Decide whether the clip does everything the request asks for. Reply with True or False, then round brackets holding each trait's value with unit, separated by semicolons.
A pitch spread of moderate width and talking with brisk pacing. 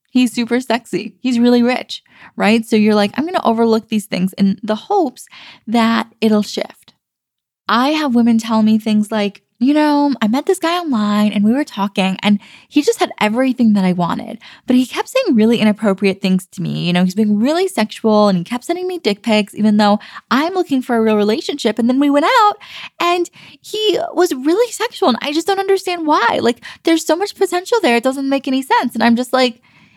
False (6.5 semitones; 215 wpm)